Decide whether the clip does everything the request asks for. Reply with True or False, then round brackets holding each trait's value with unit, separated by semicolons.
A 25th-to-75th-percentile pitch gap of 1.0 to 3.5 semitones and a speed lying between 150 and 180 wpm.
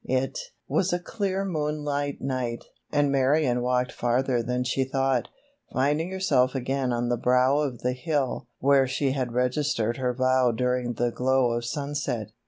True (2.5 semitones; 160 wpm)